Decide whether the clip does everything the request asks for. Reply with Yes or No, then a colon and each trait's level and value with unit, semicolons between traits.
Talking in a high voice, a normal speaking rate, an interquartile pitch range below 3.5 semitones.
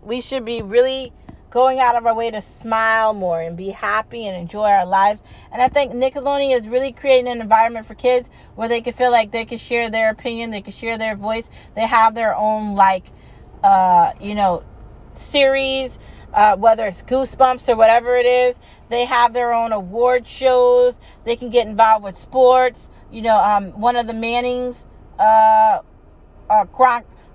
Yes: high, 235 Hz; average, 185 wpm; narrow, 2.4 semitones